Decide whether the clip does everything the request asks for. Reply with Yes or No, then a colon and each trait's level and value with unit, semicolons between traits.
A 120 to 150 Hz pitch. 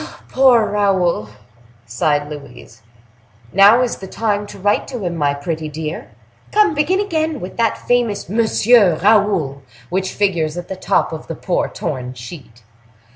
No: high, 190 Hz